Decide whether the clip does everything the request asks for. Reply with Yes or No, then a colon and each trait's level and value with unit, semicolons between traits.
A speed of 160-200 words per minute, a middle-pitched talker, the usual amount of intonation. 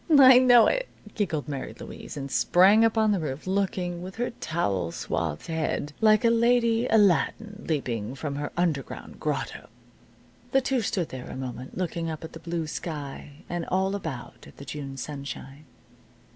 No: average, 170 wpm; medium, 170 Hz; wide, 7.3 semitones